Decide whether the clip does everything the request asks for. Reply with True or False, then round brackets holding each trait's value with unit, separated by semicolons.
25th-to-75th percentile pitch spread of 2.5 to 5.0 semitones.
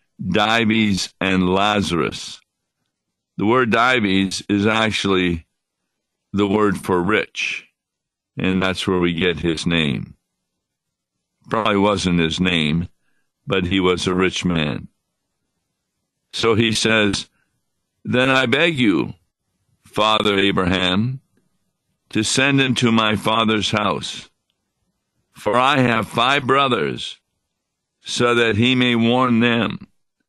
True (3.6 semitones)